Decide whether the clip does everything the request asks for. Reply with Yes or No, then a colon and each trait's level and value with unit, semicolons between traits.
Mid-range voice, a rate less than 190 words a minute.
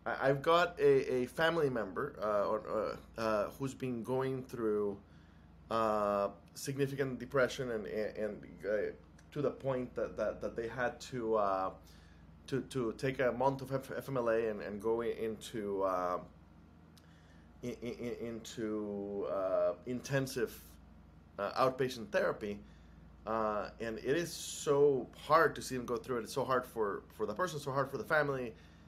No: low, 115 Hz; average, 160 wpm